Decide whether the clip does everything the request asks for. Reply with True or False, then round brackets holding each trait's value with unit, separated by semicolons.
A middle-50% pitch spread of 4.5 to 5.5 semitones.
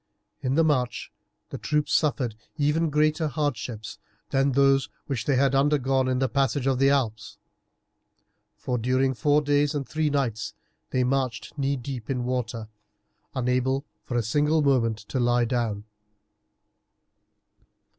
False (2.8 semitones)